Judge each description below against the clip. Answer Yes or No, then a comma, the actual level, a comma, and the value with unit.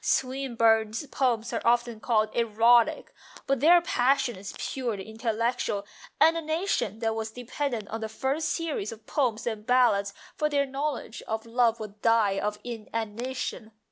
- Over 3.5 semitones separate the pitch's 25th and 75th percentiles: No, average, 3.2 semitones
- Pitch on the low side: No, high, 230 Hz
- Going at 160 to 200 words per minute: No, average, 150 wpm